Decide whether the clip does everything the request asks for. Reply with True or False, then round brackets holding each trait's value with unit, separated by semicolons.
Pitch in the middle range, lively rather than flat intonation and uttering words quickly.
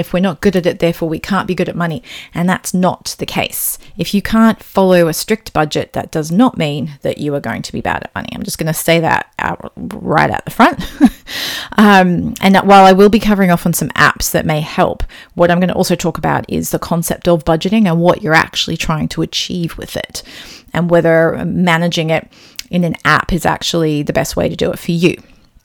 False (175 Hz; 2.6 semitones; 240 wpm)